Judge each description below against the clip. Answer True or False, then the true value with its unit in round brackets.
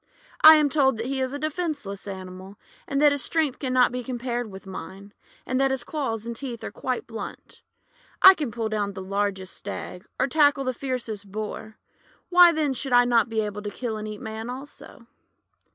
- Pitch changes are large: False (4.6 semitones)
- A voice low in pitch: False (240 Hz)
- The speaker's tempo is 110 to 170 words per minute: False (200 wpm)